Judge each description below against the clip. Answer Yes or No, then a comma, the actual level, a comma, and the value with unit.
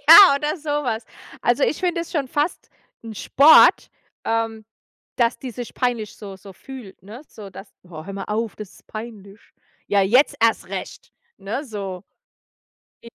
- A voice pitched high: Yes, high, 225 Hz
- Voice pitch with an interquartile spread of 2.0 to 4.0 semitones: No, average, 5.3 semitones